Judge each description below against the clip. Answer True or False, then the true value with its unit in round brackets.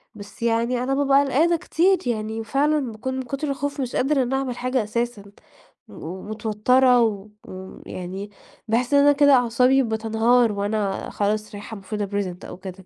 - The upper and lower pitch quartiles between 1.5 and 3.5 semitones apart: False (4.2 semitones)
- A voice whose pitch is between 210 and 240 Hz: True (235 Hz)